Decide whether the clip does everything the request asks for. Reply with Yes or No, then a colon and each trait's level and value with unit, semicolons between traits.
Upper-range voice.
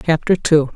No: medium, 160 Hz